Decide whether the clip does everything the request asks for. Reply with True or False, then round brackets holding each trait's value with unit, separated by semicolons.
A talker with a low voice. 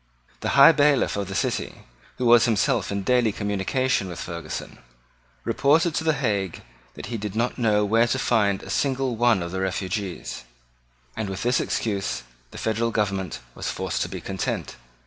True (110 Hz)